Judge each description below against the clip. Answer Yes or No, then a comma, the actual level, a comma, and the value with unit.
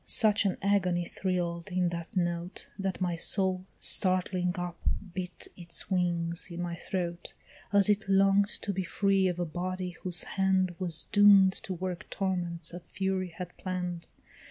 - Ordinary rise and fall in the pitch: No, narrow, 1.7 semitones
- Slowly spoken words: No, average, 155 wpm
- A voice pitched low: No, medium, 185 Hz